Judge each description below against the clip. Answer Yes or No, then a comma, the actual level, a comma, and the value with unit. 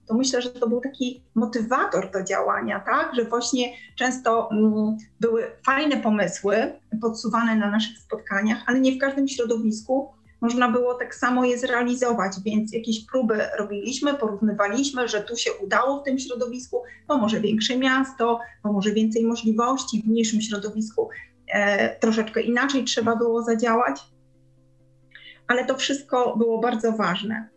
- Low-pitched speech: No, high, 235 Hz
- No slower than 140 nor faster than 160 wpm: Yes, average, 145 wpm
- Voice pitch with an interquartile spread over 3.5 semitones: No, average, 2.7 semitones